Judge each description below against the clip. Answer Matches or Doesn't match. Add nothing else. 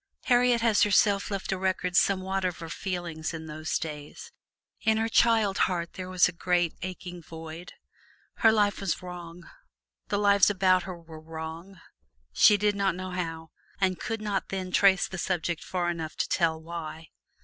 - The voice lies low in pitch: Doesn't match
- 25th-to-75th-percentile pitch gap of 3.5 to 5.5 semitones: Doesn't match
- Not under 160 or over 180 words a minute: Matches